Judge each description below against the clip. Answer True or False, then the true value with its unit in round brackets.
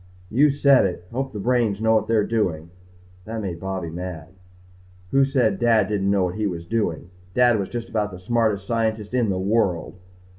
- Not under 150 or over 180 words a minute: False (190 wpm)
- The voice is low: True (105 Hz)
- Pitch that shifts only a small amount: False (4.0 semitones)